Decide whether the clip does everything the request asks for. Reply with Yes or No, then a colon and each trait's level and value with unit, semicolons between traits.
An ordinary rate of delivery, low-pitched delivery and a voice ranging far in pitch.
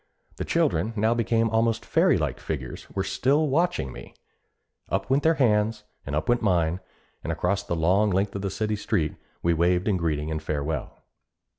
Yes: average, 175 wpm; low, 100 Hz; wide, 5.8 semitones